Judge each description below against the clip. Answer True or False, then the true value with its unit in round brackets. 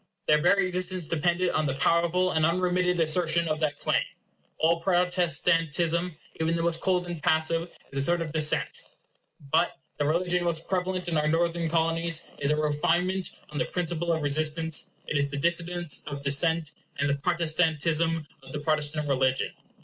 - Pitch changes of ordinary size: False (2.3 semitones)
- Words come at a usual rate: True (170 wpm)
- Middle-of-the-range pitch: True (165 Hz)